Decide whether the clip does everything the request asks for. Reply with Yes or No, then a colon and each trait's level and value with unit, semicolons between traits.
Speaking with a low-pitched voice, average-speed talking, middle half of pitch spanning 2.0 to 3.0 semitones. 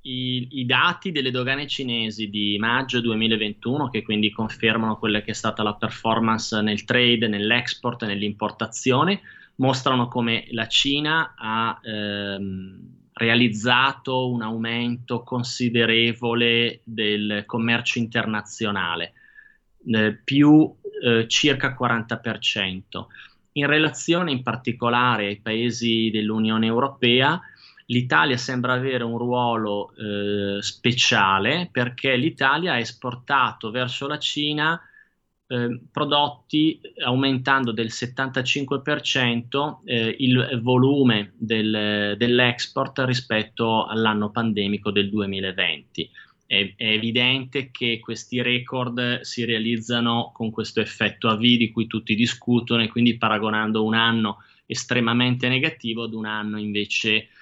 No: low, 120 Hz; slow, 110 wpm; narrow, 2.5 semitones